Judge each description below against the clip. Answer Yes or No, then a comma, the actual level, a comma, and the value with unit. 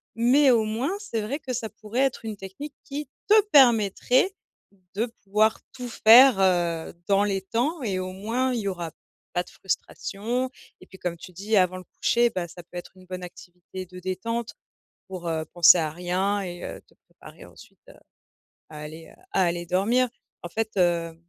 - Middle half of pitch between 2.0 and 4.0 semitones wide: No, average, 4.8 semitones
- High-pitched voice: Yes, high, 195 Hz